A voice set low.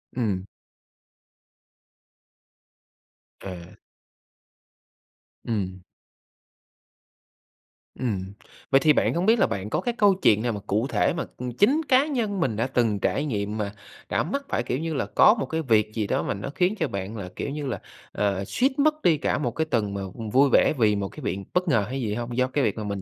Yes: low, 120 Hz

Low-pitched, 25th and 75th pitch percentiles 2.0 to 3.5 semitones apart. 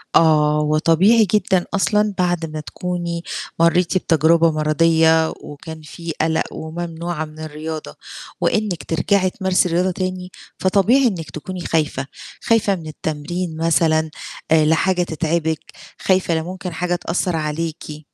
No: medium, 165 Hz; narrow, 2.5 semitones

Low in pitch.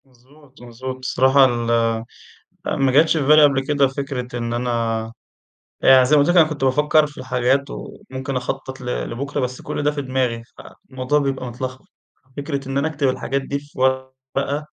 Yes: low, 130 Hz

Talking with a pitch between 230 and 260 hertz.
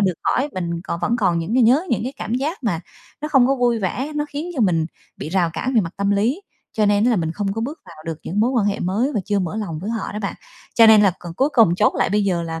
No: high, 210 Hz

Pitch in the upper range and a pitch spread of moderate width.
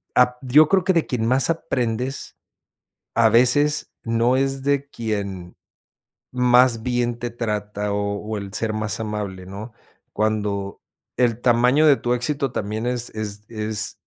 No: low, 115 Hz; average, 3.0 semitones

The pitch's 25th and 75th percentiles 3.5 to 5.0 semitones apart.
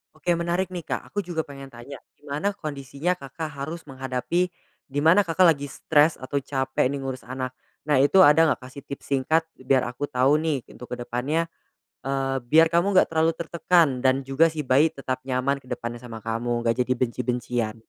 Yes: average, 3.9 semitones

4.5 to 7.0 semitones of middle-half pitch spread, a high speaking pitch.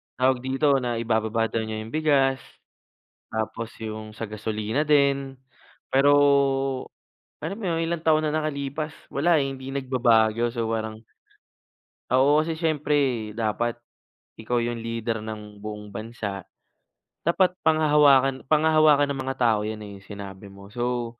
No: average, 4.8 semitones; low, 125 Hz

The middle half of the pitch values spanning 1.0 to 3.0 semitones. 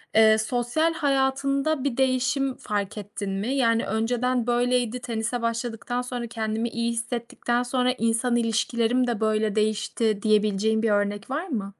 Yes: narrow, 2.4 semitones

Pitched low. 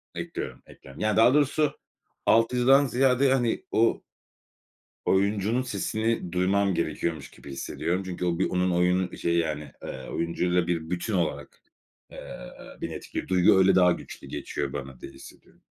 Yes: very low, 95 Hz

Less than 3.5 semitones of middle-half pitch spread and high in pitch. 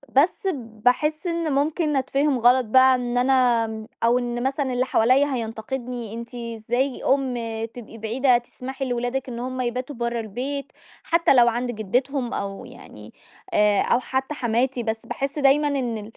Yes: narrow, 2.4 semitones; very high, 250 Hz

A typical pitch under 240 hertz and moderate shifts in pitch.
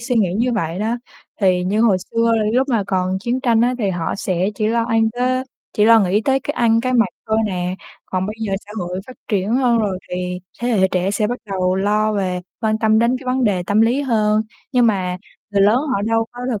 Yes: high, 215 Hz; average, 3.8 semitones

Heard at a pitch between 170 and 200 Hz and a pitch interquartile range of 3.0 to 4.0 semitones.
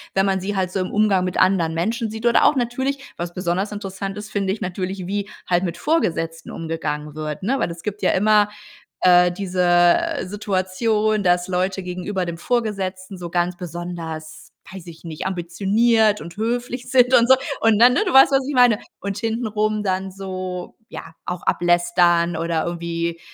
Yes: high, 190 Hz; average, 3.6 semitones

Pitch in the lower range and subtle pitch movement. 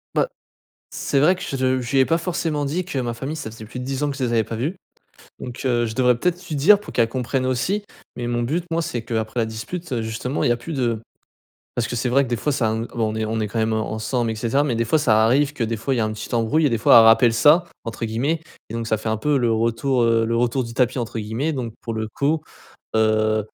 No: low, 120 Hz; average, 3.6 semitones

